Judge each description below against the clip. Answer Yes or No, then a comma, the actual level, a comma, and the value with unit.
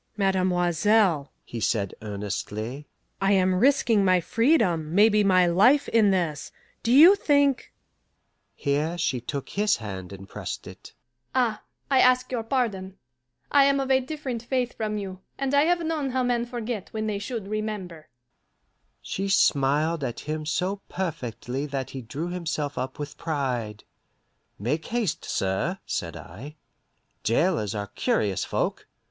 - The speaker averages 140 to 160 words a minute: Yes, average, 150 wpm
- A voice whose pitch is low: No, medium, 185 Hz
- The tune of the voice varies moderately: No, wide, 8.5 semitones